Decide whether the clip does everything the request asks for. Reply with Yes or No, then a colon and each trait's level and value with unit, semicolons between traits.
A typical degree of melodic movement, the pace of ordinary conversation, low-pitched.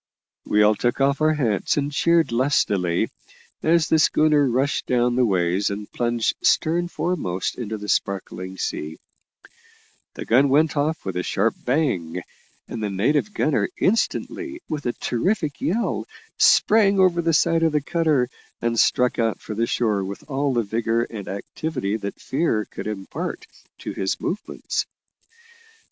No: wide, 7.0 semitones; average, 155 wpm; low, 125 Hz